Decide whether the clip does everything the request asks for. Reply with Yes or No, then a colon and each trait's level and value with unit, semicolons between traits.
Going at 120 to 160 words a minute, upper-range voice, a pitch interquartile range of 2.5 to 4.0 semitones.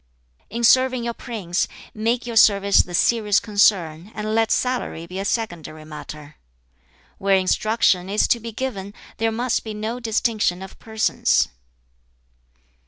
Yes: average, 140 wpm; high, 215 Hz; average, 3.5 semitones